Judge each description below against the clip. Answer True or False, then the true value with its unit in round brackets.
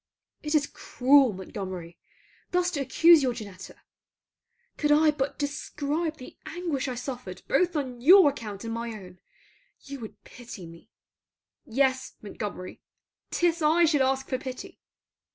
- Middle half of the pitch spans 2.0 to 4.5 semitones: False (5.1 semitones)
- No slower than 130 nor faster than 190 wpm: True (140 wpm)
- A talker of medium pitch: False (265 Hz)